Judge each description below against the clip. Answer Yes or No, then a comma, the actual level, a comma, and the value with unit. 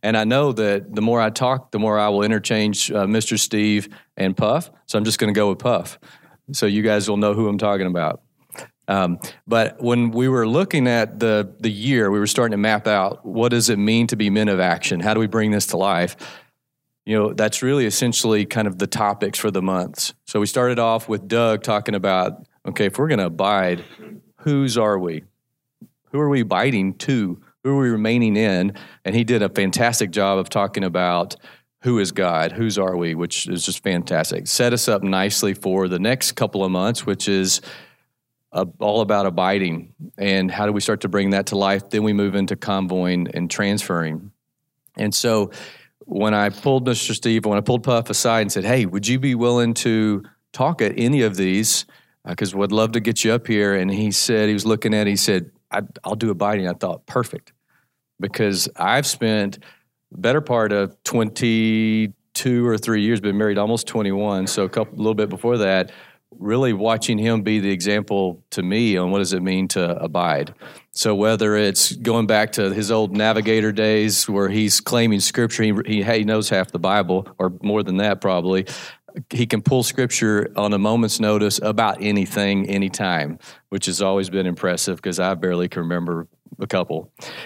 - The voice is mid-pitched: No, low, 105 Hz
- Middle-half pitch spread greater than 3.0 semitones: No, narrow, 2.6 semitones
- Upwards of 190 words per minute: Yes, average, 200 wpm